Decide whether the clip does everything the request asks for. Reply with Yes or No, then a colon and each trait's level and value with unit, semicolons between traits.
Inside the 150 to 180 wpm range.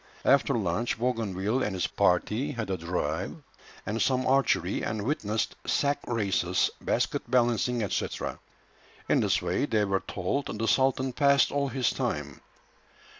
No: average, 140 wpm